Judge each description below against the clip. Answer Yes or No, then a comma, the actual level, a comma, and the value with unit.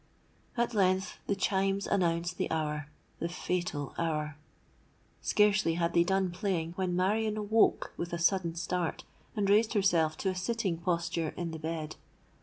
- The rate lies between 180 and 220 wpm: No, average, 150 wpm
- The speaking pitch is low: No, medium, 180 Hz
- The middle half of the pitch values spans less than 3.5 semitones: Yes, average, 3.0 semitones